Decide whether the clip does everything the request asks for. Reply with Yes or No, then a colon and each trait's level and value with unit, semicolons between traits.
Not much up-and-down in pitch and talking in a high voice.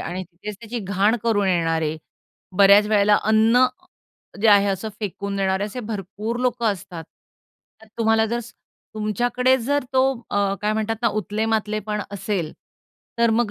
Yes: narrow, 2.3 semitones; high, 210 Hz